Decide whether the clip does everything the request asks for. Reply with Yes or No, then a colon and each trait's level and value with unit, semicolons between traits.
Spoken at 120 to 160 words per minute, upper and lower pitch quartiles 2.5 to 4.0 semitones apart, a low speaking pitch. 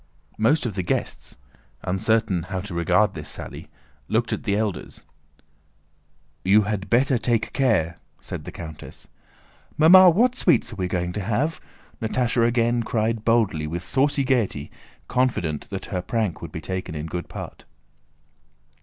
No: average, 150 wpm; average, 5.0 semitones; low, 110 Hz